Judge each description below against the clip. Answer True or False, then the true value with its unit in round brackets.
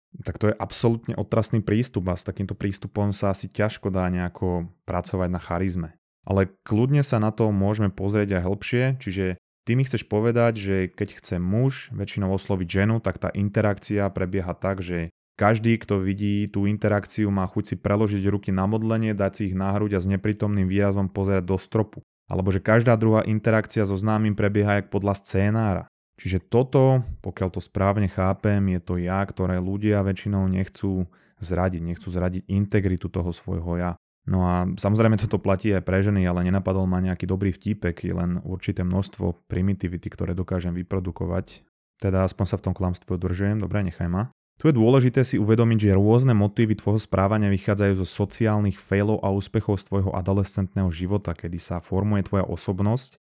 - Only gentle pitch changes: True (2.2 semitones)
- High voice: False (100 Hz)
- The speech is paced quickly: True (175 wpm)